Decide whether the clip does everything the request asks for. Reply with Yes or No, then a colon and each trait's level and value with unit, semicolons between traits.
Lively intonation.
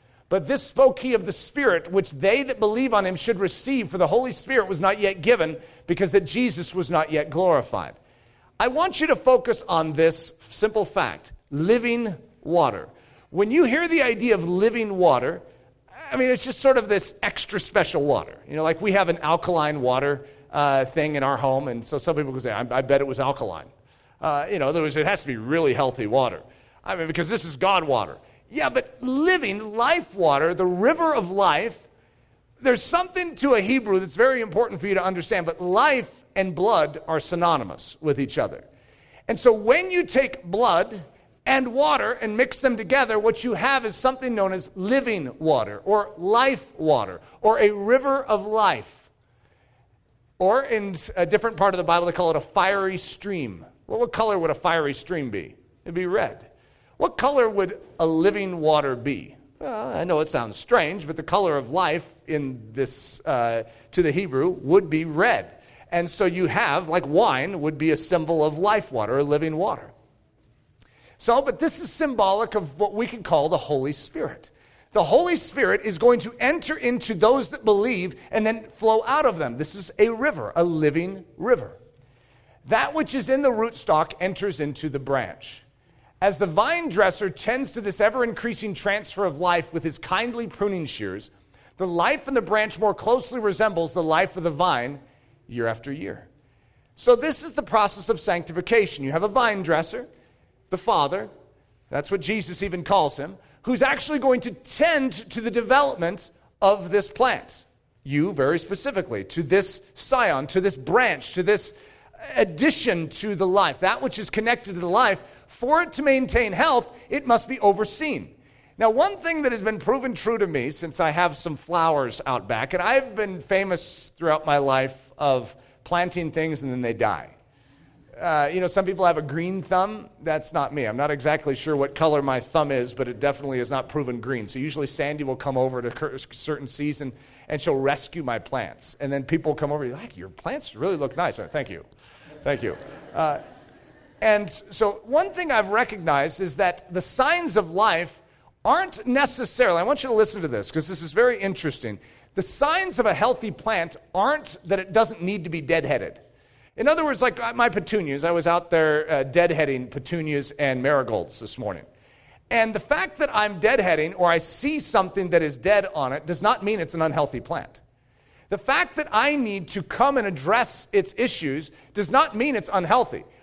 Yes: wide, 7.2 semitones